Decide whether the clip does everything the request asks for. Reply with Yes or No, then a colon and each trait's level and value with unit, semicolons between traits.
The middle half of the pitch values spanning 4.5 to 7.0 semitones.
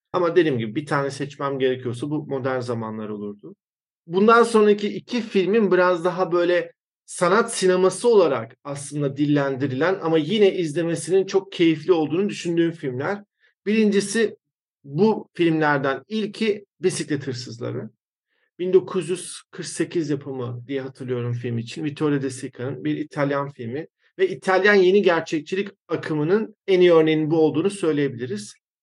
Yes: wide, 5.4 semitones